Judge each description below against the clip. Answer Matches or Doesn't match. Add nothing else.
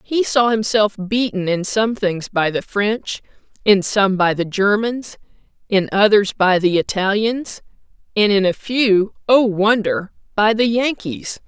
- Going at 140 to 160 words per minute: Matches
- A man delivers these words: Doesn't match